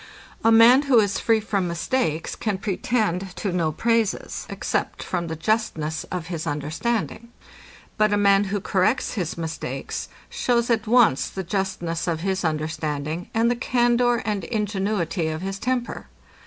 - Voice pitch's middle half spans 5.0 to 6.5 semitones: Yes, average, 5.3 semitones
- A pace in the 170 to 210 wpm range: No, average, 155 wpm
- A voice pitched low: No, high, 195 Hz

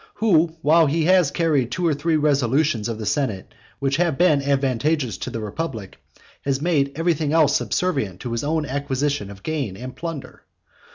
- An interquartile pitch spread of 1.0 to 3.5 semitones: No, average, 4.2 semitones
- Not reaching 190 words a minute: Yes, average, 175 wpm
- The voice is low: No, medium, 145 Hz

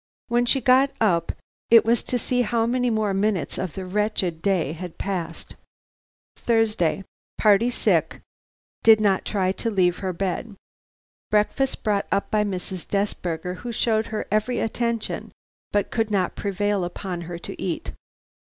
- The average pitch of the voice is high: Yes, high, 205 Hz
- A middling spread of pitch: Yes, average, 3.5 semitones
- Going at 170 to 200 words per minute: No, average, 155 wpm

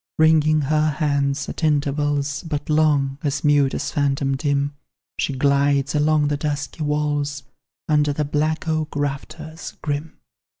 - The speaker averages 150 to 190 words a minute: No, slow, 135 wpm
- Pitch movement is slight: Yes, narrow, 1.4 semitones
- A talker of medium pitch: Yes, medium, 145 Hz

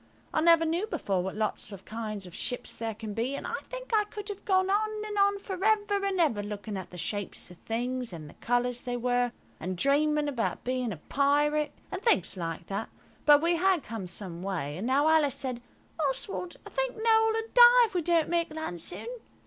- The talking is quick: Yes, fast, 215 wpm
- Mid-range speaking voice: No, very high, 280 Hz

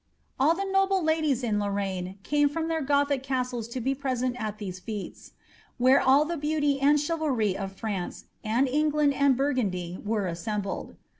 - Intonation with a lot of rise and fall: Yes, wide, 5.8 semitones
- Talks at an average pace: Yes, average, 165 wpm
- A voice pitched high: Yes, very high, 260 Hz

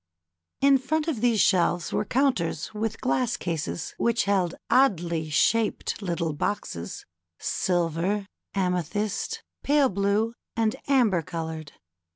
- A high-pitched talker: Yes, high, 200 Hz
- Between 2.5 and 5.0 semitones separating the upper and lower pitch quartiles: No, wide, 5.5 semitones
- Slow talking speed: Yes, slow, 120 wpm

